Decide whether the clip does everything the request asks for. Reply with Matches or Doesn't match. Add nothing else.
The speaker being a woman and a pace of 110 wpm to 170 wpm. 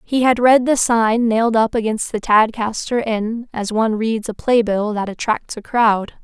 Doesn't match